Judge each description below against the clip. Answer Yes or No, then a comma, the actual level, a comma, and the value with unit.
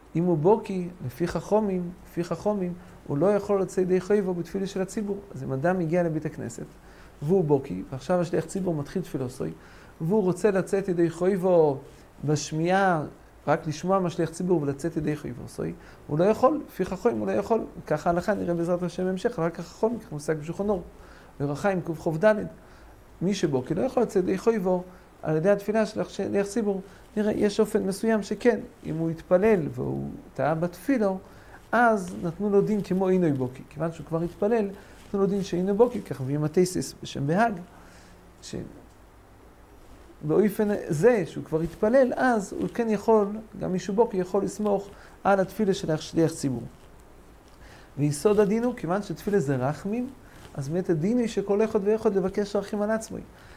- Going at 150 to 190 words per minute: Yes, average, 155 wpm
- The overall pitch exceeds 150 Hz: Yes, medium, 185 Hz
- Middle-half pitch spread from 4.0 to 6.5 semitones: Yes, average, 4.5 semitones